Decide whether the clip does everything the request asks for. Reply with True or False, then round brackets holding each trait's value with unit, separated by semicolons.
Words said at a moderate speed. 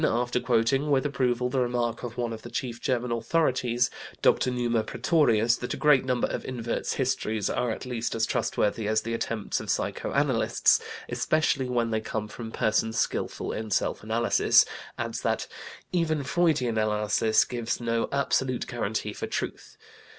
True (165 wpm)